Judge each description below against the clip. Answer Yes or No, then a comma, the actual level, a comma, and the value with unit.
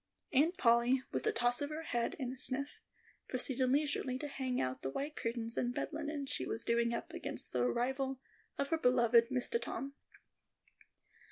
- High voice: Yes, very high, 255 Hz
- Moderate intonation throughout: Yes, average, 3.1 semitones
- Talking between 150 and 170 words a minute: No, average, 180 wpm